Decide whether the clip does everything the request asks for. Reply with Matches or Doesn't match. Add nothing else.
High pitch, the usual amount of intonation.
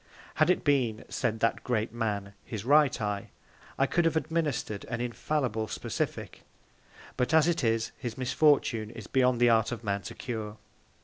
Doesn't match